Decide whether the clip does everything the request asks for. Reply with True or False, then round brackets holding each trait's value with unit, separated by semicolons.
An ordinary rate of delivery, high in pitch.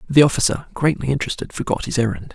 False (180 wpm; 130 Hz)